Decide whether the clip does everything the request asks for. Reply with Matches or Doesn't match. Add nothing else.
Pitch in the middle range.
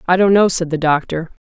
Matches